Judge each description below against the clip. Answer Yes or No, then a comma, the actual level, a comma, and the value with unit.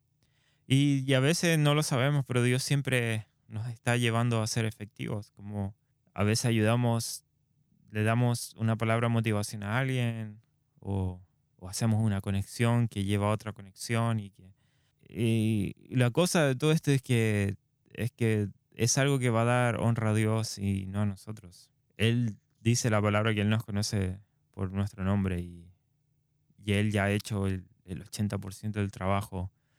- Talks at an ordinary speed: Yes, average, 170 wpm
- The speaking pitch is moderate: No, low, 110 Hz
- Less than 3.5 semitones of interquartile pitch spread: No, average, 4.0 semitones